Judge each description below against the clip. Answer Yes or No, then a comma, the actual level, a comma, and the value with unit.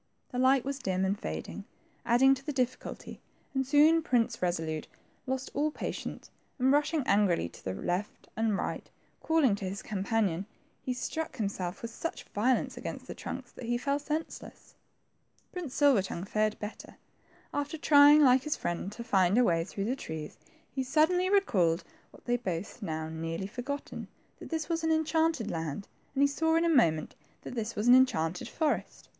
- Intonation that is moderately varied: No, wide, 7.1 semitones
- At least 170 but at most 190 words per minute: Yes, average, 180 wpm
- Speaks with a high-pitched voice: Yes, high, 245 Hz